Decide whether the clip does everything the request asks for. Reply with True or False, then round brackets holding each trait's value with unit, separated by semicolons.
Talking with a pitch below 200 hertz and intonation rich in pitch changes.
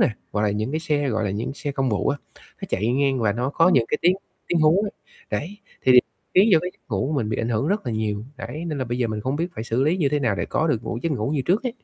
True (135 Hz; 6.0 semitones)